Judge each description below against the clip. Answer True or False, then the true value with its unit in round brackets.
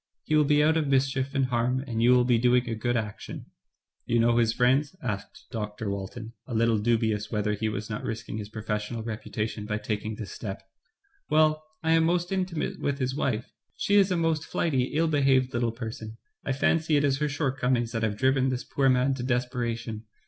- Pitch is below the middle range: True (125 Hz)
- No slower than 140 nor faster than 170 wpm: False (205 wpm)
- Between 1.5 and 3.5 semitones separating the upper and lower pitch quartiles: False (3.9 semitones)